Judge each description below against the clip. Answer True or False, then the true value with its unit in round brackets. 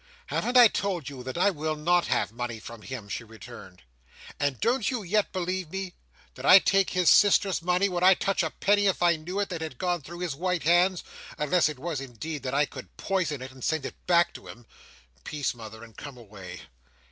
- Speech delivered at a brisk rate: True (215 wpm)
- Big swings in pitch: True (6.1 semitones)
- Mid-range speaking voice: True (165 Hz)